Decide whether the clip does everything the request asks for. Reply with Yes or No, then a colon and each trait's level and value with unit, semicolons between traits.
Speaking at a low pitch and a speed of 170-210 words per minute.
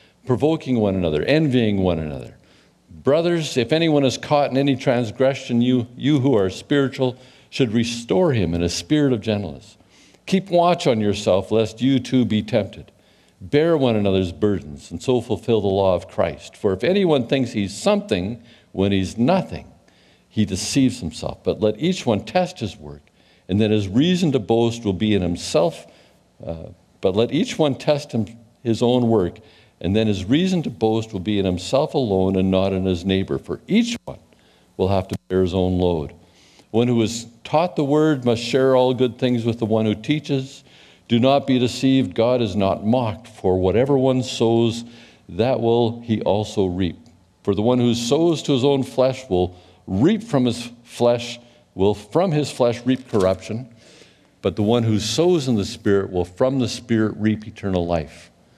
Yes: low, 115 Hz; average, 185 wpm